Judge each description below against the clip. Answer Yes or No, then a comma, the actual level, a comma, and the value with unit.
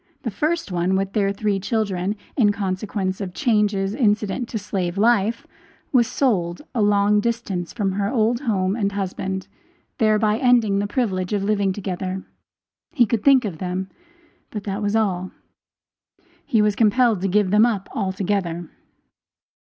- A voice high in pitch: Yes, high, 205 Hz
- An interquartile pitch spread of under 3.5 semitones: Yes, narrow, 2.6 semitones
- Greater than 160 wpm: No, average, 150 wpm